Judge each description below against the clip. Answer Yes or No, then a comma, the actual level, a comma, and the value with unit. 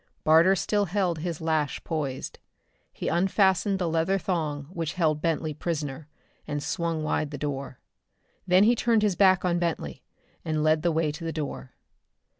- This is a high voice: No, medium, 165 Hz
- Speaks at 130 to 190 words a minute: Yes, average, 165 wpm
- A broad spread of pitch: No, average, 3.2 semitones